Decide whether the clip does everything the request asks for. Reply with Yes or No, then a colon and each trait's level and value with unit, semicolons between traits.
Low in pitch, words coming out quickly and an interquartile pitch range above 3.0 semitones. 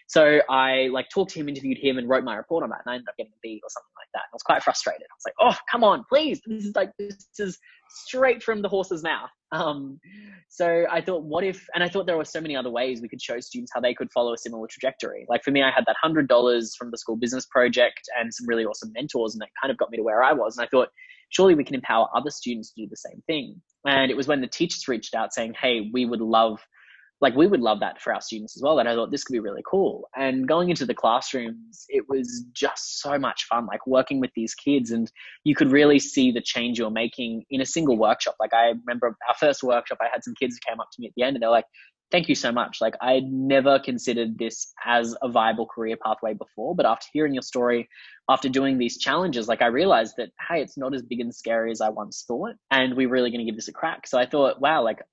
Yes: low, 130 Hz; fast, 270 wpm; average, 4.4 semitones